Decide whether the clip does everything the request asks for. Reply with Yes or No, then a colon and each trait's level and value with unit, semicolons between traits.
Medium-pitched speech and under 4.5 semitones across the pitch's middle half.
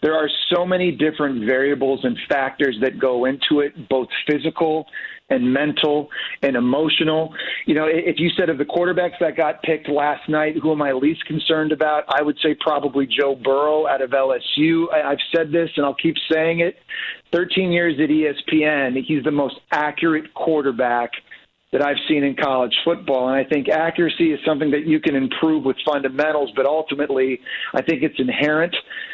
Yes: medium, 155 Hz; average, 2.7 semitones